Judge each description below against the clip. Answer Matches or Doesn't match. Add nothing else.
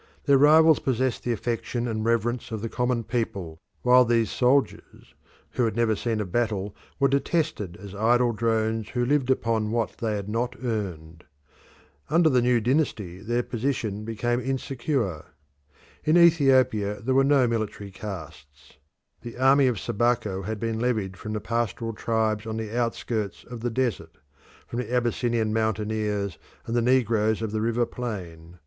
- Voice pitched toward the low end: Matches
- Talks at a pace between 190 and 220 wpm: Doesn't match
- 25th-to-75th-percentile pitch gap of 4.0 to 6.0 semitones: Doesn't match